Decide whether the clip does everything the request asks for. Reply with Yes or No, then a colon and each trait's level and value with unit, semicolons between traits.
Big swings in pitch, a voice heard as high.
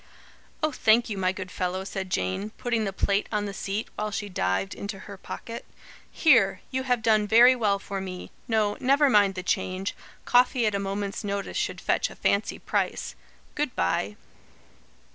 No: average, 3.1 semitones; high, 205 Hz